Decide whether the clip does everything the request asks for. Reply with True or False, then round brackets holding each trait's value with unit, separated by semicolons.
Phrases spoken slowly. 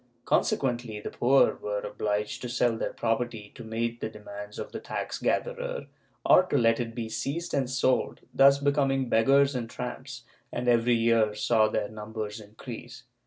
False (165 wpm)